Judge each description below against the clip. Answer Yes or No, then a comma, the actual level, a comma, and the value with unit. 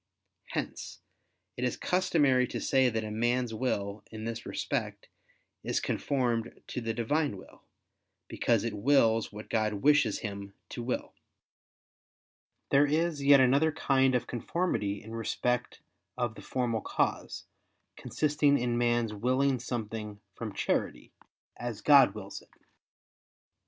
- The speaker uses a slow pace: Yes, slow, 130 wpm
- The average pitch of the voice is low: Yes, low, 120 Hz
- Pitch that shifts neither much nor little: Yes, average, 3.8 semitones